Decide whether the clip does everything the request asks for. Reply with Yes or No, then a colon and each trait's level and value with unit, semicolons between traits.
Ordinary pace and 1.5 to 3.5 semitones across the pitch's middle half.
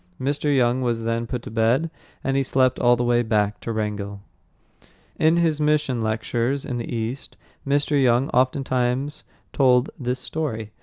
Yes: average, 160 wpm; average, 3.2 semitones